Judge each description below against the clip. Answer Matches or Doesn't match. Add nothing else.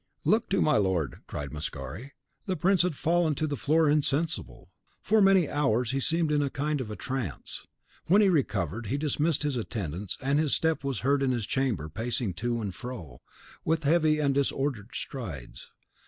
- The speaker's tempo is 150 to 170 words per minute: Doesn't match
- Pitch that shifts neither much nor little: Doesn't match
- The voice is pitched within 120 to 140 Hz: Matches